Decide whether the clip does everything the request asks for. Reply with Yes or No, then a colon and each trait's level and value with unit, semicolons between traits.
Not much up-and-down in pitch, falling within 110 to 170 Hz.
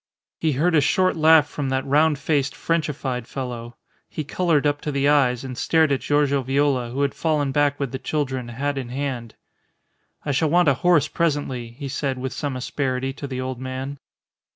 Yes: narrow, 2.3 semitones; medium, 140 Hz